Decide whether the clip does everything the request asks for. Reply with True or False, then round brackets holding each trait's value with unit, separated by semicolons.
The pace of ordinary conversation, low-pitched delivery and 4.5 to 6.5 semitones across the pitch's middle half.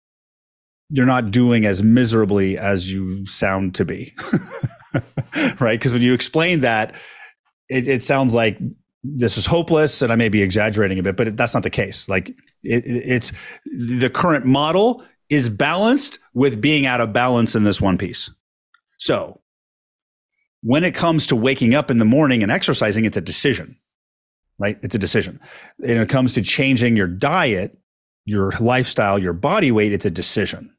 True (170 wpm; 115 Hz; 4.8 semitones)